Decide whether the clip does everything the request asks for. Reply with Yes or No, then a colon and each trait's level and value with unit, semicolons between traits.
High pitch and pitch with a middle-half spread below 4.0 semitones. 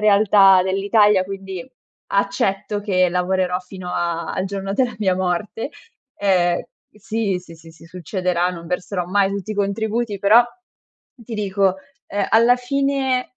Yes: high, 195 Hz; narrow, 2.6 semitones